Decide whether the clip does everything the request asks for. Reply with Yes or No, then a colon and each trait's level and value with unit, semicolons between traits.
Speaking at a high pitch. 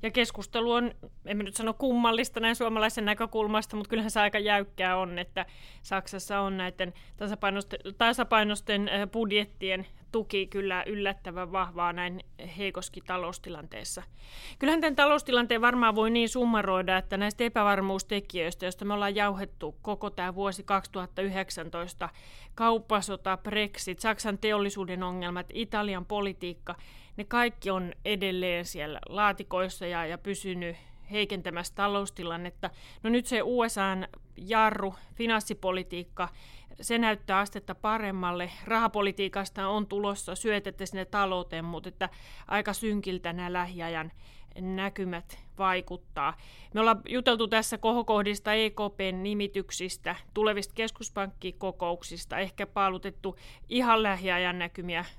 Yes: high, 195 Hz